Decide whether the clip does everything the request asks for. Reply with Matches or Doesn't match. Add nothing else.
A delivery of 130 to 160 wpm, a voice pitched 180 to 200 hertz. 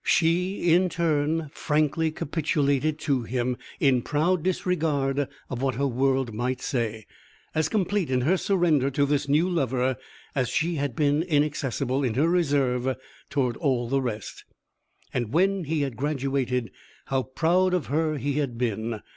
Doesn't match